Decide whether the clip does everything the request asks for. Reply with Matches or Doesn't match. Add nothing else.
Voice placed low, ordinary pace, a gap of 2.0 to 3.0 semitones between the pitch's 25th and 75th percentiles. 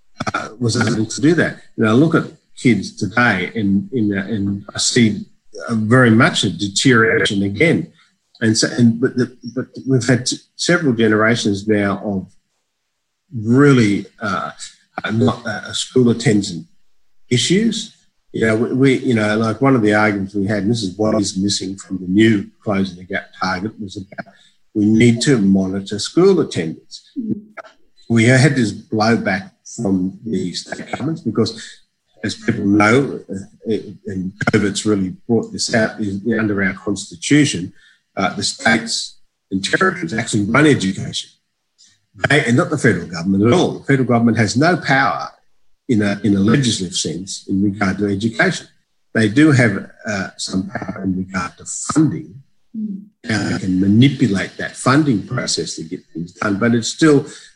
Doesn't match